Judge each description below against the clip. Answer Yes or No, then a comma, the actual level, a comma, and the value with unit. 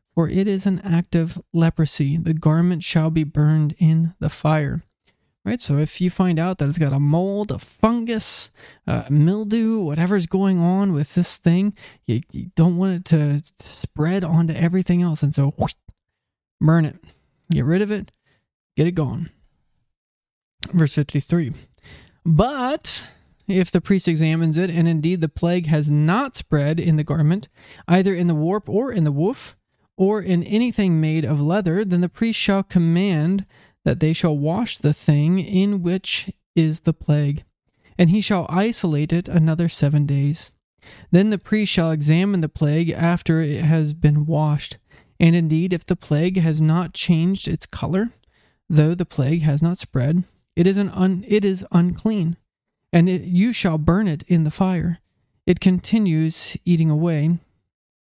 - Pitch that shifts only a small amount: No, average, 3.1 semitones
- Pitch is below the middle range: No, medium, 170 Hz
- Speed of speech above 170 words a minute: No, average, 165 wpm